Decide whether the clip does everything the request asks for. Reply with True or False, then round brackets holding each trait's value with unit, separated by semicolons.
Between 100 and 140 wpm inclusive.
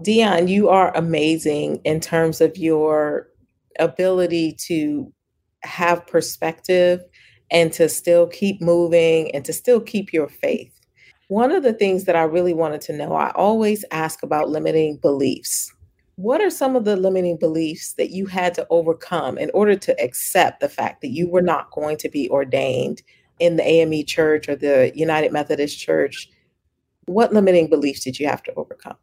False (170 wpm)